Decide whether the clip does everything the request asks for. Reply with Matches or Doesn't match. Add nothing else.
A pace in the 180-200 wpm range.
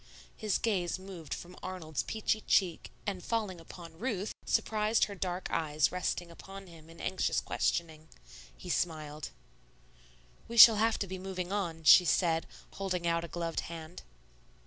Doesn't match